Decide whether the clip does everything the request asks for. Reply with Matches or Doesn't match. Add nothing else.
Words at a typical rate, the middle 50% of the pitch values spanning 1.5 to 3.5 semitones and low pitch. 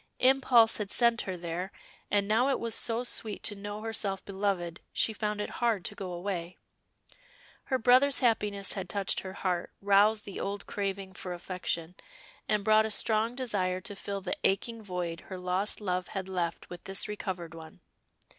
Doesn't match